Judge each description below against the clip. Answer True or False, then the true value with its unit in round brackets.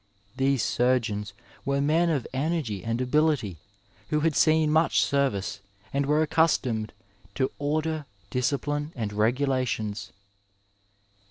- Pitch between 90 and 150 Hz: True (140 Hz)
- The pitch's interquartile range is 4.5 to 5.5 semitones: True (5.0 semitones)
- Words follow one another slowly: True (110 wpm)